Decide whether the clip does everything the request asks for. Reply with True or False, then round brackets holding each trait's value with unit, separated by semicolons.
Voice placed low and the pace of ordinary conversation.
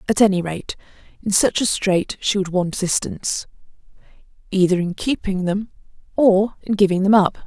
False (195 Hz; 160 wpm)